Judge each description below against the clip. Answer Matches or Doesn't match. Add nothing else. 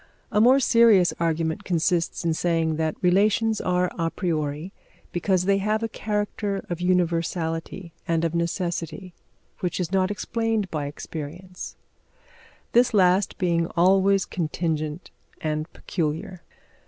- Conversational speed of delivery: Doesn't match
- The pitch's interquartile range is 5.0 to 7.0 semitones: Doesn't match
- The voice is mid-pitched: Matches